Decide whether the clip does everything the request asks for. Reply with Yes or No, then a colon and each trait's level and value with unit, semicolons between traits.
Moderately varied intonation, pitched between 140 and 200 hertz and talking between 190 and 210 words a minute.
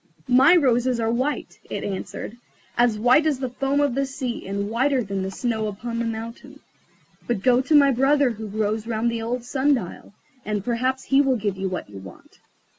No: average, 3.8 semitones; high, 235 Hz; average, 200 wpm